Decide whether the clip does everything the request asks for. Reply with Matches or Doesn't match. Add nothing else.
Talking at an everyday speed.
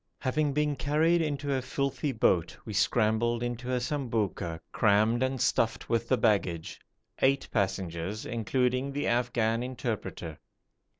Doesn't match